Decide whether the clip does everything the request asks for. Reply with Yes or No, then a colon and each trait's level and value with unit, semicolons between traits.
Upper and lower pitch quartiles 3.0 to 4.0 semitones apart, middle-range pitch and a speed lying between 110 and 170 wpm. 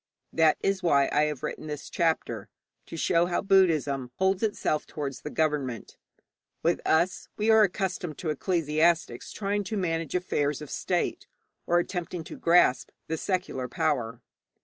Yes: average, 3.6 semitones; medium, 165 Hz; average, 150 wpm